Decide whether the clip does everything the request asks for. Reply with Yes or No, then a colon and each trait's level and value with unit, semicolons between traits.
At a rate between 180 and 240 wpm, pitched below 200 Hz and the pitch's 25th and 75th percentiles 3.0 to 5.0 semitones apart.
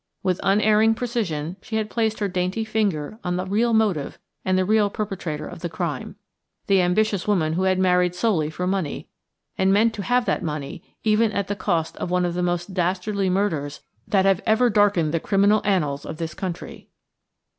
Yes: average, 190 wpm; high, 190 Hz; average, 3.3 semitones